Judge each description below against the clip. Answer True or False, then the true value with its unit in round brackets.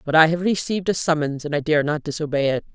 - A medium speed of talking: False (260 wpm)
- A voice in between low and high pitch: True (155 Hz)